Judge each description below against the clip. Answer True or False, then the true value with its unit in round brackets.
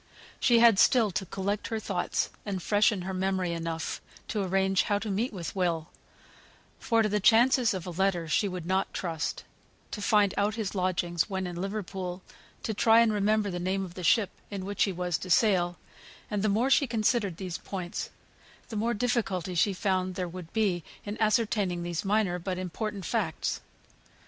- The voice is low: False (195 Hz)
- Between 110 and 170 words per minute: False (185 wpm)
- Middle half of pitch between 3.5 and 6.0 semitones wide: False (2.9 semitones)